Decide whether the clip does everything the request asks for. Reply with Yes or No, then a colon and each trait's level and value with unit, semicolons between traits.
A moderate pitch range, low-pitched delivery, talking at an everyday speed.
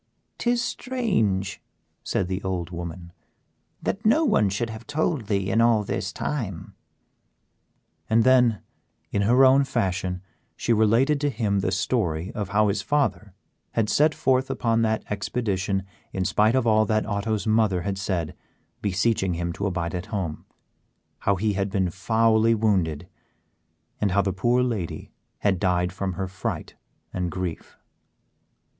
Yes: average, 3.7 semitones; low, 100 Hz; average, 150 wpm